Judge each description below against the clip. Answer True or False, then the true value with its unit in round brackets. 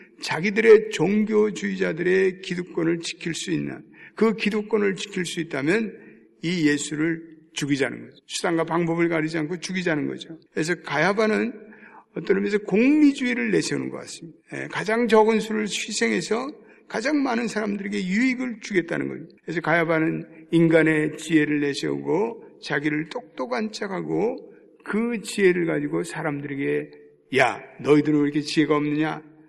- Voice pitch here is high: False (175 Hz)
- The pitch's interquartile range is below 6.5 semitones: True (5.5 semitones)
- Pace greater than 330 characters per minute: True (340 characters per minute)